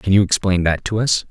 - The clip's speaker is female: No, male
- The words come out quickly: Yes, fast, 275 wpm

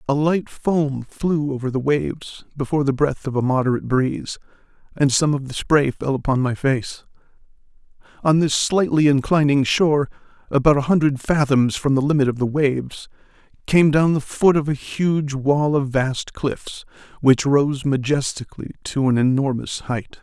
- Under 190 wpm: Yes, average, 165 wpm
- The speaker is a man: Yes, male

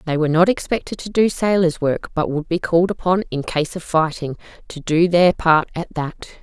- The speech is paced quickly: Yes, fast, 215 wpm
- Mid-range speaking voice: Yes, medium, 170 Hz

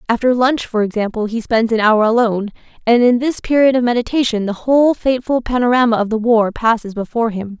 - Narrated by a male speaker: No, female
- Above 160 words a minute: Yes, average, 195 wpm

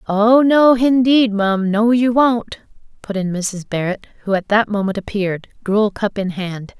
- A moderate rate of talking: Yes, average, 170 wpm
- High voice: Yes, high, 210 Hz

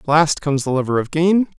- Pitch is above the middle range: No, medium, 155 Hz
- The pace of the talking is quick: Yes, fast, 225 wpm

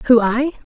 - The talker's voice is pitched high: Yes, high, 245 Hz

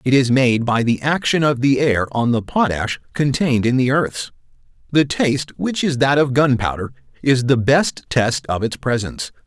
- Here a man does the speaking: Yes, male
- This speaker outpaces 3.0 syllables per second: No, 2.9 syllables/s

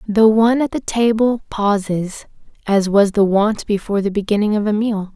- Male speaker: No, female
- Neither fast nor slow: Yes, average, 185 wpm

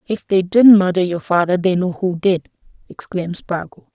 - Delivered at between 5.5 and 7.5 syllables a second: No, 5.0 syllables/s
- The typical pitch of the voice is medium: Yes, medium, 180 Hz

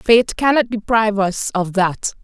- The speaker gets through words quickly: No, average, 160 wpm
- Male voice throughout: No, female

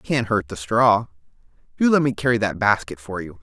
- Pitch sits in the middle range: No, low, 110 Hz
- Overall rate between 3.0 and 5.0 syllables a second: No, 5.6 syllables/s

